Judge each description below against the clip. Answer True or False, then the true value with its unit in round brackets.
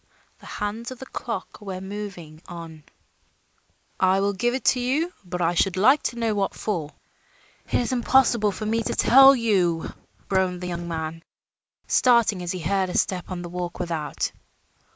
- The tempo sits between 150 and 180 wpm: True (175 wpm)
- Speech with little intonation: False (4.8 semitones)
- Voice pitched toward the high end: True (195 Hz)